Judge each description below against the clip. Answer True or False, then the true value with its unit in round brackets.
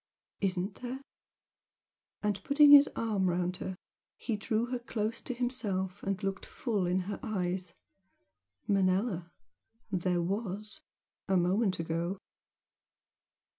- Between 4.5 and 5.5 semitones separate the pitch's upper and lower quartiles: False (3.6 semitones)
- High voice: True (195 Hz)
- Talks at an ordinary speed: False (115 wpm)